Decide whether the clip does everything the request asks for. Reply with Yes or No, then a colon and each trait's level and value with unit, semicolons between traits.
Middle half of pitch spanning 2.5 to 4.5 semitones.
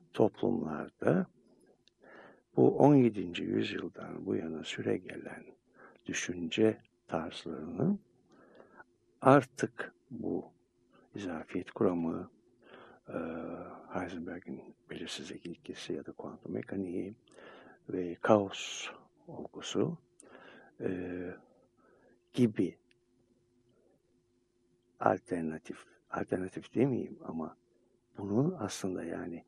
No: average, 5.2 semitones